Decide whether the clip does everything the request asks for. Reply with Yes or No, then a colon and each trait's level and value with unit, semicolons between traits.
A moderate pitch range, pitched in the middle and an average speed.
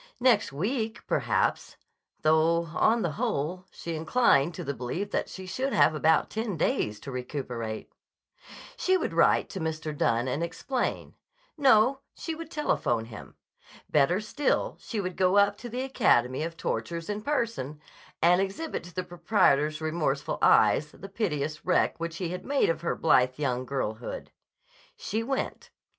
No: wide, 7.0 semitones; medium, 170 Hz; average, 155 wpm